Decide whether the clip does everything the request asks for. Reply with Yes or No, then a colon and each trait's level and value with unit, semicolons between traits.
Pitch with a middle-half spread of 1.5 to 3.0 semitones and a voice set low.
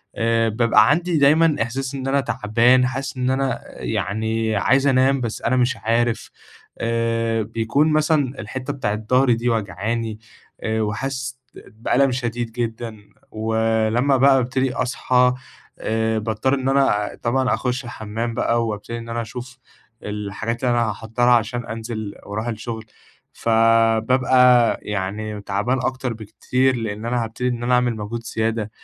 Yes: narrow, 2.5 semitones; low, 115 Hz